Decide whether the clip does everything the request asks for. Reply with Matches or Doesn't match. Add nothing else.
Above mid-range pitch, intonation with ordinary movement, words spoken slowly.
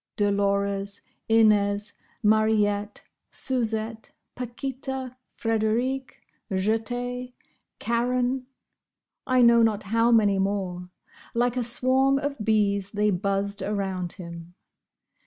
Matches